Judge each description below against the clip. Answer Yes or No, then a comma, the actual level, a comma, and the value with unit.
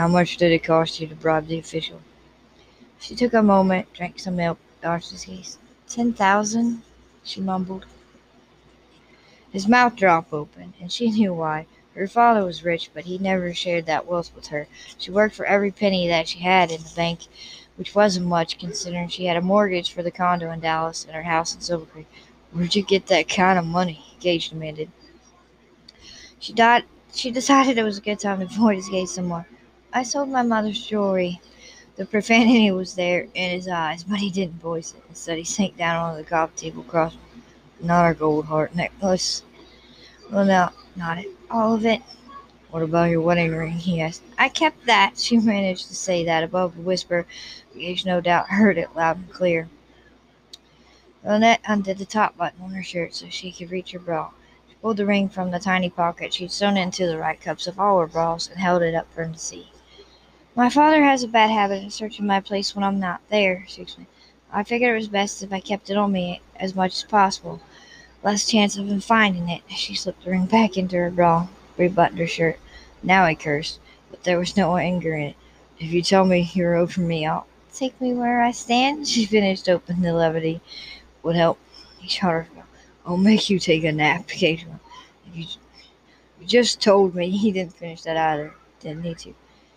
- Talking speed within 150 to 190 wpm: No, fast, 205 wpm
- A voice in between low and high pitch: Yes, medium, 180 Hz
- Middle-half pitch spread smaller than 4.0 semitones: Yes, average, 3.3 semitones